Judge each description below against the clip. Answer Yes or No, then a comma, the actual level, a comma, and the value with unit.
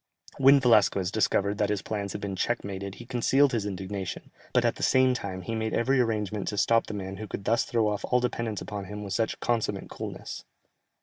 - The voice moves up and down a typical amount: Yes, average, 3.0 semitones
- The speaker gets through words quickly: Yes, fast, 220 wpm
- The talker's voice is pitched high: No, low, 105 Hz